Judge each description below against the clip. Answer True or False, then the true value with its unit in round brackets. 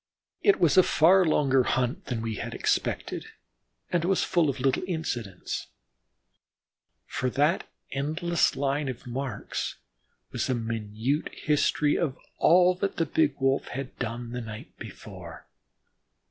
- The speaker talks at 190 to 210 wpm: False (135 wpm)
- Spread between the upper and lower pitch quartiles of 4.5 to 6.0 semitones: True (4.8 semitones)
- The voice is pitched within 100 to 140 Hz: True (135 Hz)